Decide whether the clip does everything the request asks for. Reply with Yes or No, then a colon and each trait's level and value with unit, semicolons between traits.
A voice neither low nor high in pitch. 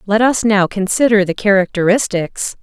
No: high, 205 Hz